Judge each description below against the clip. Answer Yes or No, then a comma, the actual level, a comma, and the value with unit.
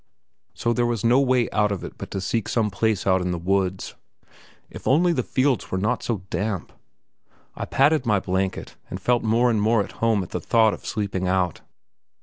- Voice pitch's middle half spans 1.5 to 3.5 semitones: No, average, 4.0 semitones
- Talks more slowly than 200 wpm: No, fast, 205 wpm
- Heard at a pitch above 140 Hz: No, low, 105 Hz